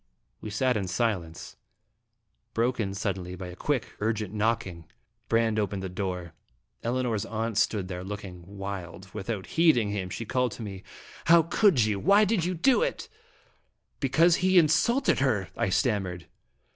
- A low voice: Yes, low, 105 Hz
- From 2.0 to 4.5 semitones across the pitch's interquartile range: No, average, 5.2 semitones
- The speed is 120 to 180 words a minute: Yes, average, 160 wpm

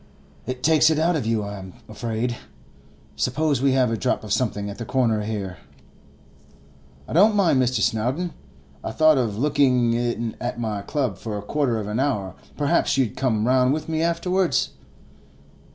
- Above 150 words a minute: Yes, average, 170 wpm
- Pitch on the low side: Yes, low, 125 Hz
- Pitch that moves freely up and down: No, average, 4.9 semitones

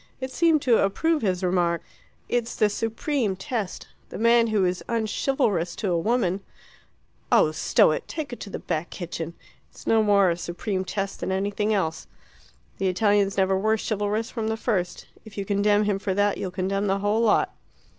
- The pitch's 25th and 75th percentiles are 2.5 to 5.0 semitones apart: Yes, average, 2.9 semitones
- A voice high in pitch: Yes, high, 205 Hz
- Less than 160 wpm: No, average, 185 wpm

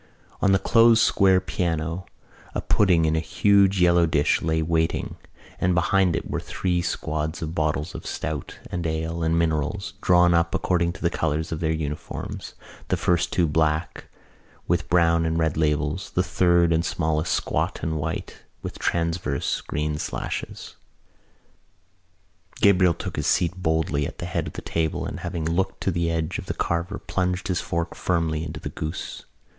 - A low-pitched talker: Yes, very low, 85 Hz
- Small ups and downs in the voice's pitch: Yes, narrow, 2.1 semitones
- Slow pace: No, average, 170 wpm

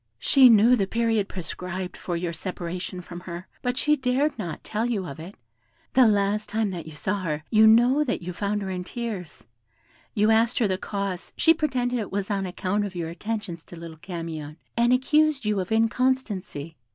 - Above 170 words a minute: Yes, average, 195 wpm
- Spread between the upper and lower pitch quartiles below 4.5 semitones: No, average, 4.8 semitones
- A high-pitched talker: Yes, high, 200 Hz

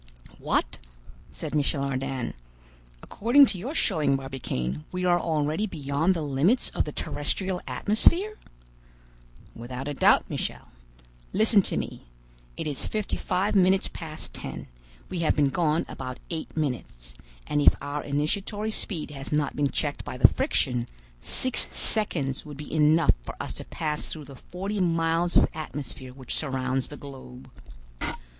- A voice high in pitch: No, medium, 150 Hz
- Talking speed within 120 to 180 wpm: Yes, average, 150 wpm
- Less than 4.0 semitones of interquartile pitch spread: No, average, 5.1 semitones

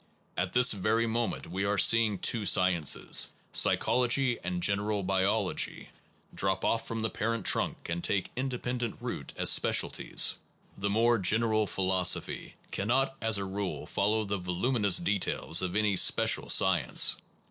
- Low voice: Yes, low, 105 Hz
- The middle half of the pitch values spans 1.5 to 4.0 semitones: Yes, average, 3.3 semitones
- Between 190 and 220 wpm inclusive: No, average, 145 wpm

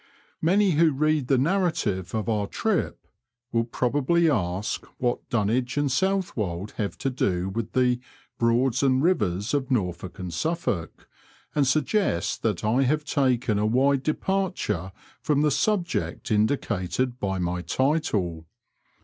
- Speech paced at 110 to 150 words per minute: Yes, slow, 135 wpm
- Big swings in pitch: Yes, wide, 6.7 semitones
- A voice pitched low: Yes, low, 125 Hz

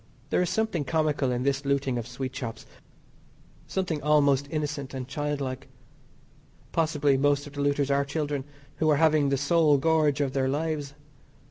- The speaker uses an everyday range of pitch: No, narrow, 1.9 semitones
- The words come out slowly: No, average, 165 wpm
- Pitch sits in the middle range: Yes, medium, 145 Hz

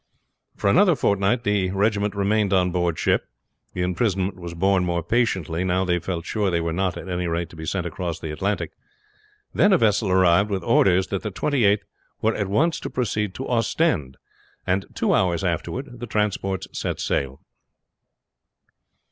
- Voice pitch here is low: Yes, very low, 95 Hz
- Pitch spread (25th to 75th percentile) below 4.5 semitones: Yes, average, 3.2 semitones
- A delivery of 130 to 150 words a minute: No, average, 180 wpm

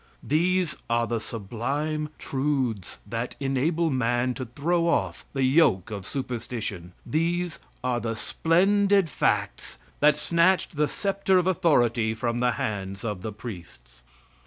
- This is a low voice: Yes, low, 130 Hz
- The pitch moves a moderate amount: No, wide, 6.5 semitones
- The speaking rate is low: Yes, slow, 130 wpm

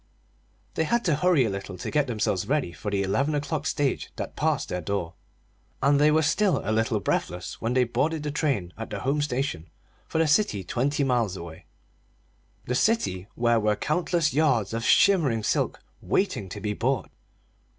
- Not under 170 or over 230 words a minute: Yes, average, 180 wpm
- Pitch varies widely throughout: Yes, wide, 6.6 semitones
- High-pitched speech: No, low, 130 Hz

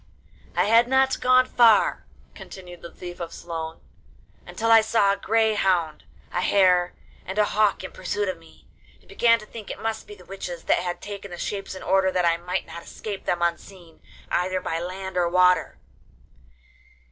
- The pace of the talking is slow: No, average, 185 wpm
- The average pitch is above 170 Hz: Yes, high, 190 Hz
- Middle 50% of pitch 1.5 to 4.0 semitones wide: Yes, average, 3.3 semitones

